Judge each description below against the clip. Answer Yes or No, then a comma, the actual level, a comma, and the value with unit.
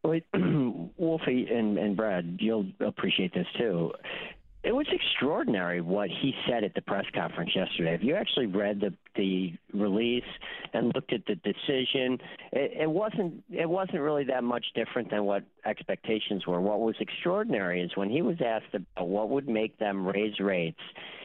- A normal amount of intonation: No, wide, 5.8 semitones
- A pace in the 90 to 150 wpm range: No, average, 170 wpm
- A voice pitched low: Yes, low, 110 Hz